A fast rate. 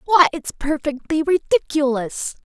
No: slow, 95 wpm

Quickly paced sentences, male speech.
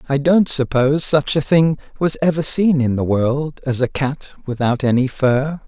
No: average, 190 wpm; male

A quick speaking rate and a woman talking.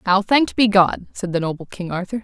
Yes: fast, 240 wpm; female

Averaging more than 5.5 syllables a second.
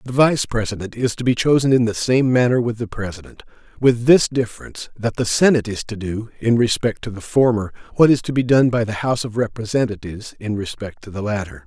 Yes: 6.0 syllables/s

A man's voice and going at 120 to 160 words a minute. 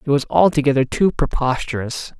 Yes: male; slow, 135 wpm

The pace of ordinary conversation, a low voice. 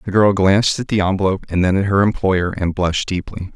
No: fast, 235 wpm; very low, 95 Hz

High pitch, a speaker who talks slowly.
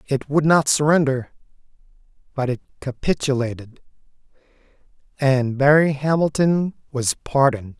No: medium, 140 Hz; slow, 90 wpm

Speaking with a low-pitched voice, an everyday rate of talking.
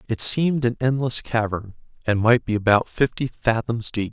Yes: low, 115 Hz; average, 175 wpm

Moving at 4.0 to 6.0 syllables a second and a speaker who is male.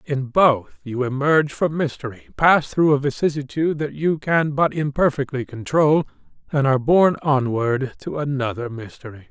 Yes: 4.9 syllables/s; male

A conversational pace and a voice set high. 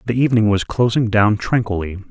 No: average, 170 wpm; low, 110 Hz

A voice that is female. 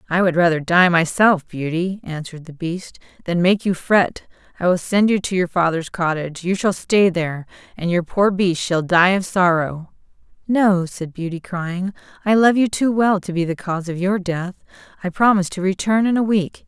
Yes: female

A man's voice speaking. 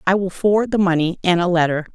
No: female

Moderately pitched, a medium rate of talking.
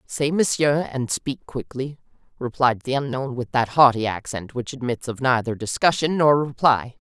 No: low, 130 Hz; average, 160 wpm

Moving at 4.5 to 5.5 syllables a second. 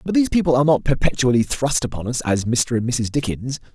No: 6.3 syllables/s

